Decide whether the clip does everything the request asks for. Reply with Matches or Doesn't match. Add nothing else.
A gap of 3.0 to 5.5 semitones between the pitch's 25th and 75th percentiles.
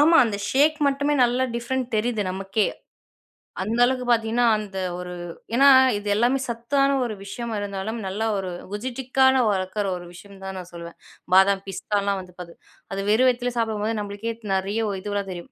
Matches